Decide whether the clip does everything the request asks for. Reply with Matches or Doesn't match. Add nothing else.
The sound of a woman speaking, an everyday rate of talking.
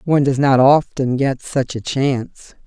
Matches